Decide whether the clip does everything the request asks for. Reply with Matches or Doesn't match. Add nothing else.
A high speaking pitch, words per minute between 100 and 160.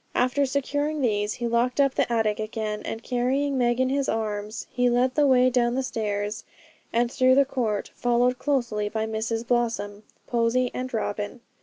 Doesn't match